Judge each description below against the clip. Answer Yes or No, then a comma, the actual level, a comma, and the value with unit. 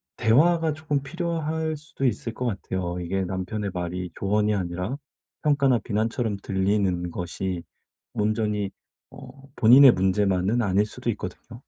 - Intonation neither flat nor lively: No, wide, 5.8 semitones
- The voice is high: No, low, 105 Hz